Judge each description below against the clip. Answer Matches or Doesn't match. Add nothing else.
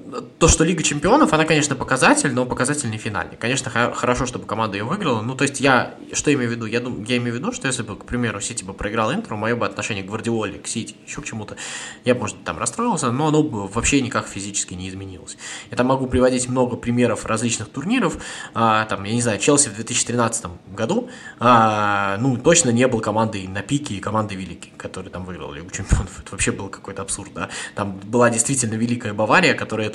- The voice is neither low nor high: Doesn't match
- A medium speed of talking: Doesn't match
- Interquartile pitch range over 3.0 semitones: Matches